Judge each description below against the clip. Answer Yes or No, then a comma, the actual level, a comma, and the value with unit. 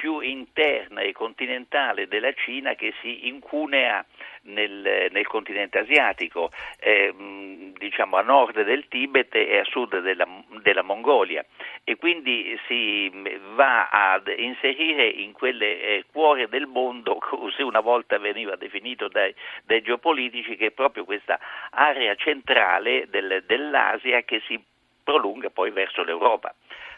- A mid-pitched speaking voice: No, low, 125 Hz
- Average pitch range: No, wide, 7.2 semitones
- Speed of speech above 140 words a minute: No, average, 130 wpm